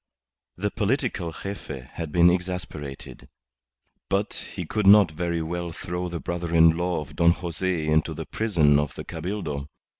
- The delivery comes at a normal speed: Yes, average, 155 wpm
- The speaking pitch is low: Yes, very low, 85 Hz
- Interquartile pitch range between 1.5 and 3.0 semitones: Yes, narrow, 2.6 semitones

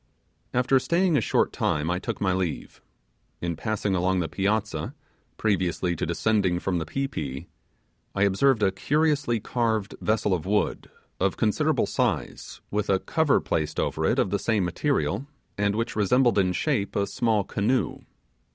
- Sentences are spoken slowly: No, average, 160 wpm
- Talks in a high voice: No, low, 100 Hz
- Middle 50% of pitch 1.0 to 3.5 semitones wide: No, average, 4.4 semitones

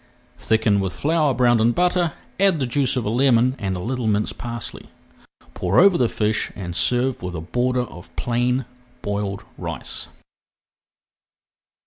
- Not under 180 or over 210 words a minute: No, average, 150 wpm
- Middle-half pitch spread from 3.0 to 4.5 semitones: Yes, average, 4.2 semitones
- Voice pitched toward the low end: Yes, low, 120 Hz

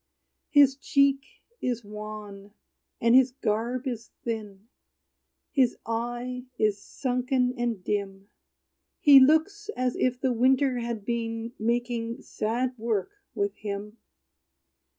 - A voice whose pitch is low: No, high, 240 Hz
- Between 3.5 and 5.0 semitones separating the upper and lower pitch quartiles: No, average, 3.1 semitones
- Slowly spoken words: Yes, slow, 110 wpm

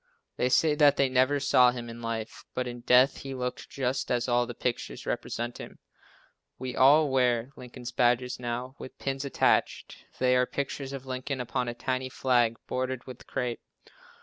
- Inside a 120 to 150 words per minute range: No, average, 175 wpm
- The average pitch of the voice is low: Yes, low, 125 Hz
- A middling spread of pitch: No, narrow, 1.4 semitones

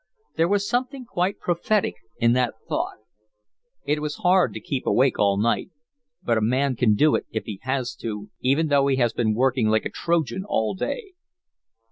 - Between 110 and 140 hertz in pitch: Yes, low, 135 Hz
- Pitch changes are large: Yes, wide, 6.9 semitones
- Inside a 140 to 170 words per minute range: No, average, 185 wpm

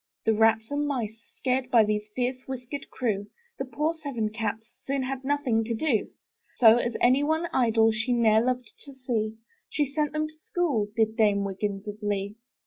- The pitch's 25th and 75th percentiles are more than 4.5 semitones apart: No, average, 3.7 semitones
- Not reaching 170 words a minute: No, average, 185 wpm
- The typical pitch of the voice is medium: No, high, 235 Hz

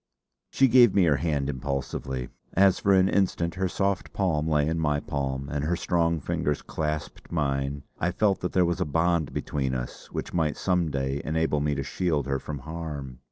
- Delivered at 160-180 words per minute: No, average, 195 wpm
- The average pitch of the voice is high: No, very low, 75 Hz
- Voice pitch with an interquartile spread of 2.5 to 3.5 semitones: No, average, 3.9 semitones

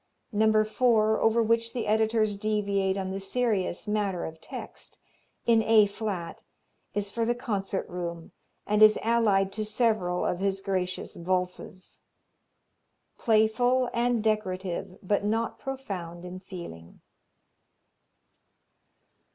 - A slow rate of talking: Yes, slow, 120 wpm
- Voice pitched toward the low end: No, high, 210 Hz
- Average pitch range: Yes, average, 3.0 semitones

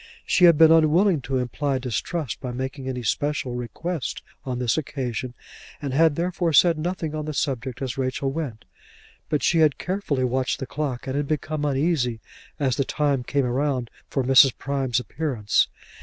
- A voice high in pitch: No, medium, 140 Hz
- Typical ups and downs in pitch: Yes, average, 3.3 semitones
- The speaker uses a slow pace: No, average, 170 wpm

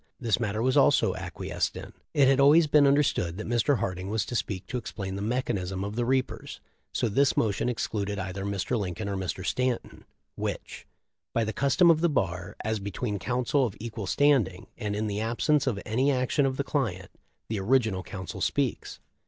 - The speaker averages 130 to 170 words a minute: No, average, 195 wpm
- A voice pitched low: Yes, low, 110 Hz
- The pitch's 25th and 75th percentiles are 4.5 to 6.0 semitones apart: Yes, average, 4.8 semitones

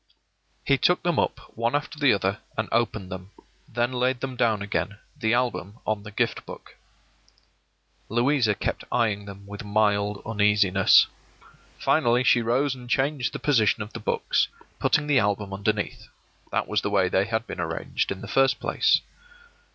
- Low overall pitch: Yes, low, 110 Hz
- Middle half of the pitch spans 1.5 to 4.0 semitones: Yes, average, 3.6 semitones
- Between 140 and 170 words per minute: Yes, average, 165 wpm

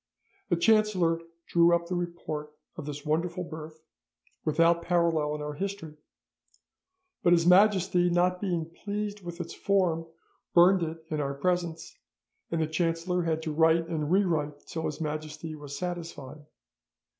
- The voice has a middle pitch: Yes, medium, 165 Hz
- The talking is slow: No, average, 145 wpm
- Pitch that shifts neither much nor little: No, narrow, 2.3 semitones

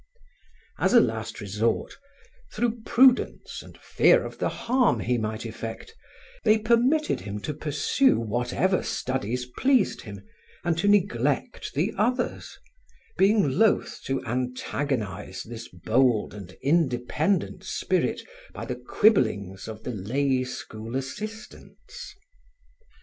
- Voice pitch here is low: Yes, low, 130 Hz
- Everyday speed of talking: No, slow, 115 wpm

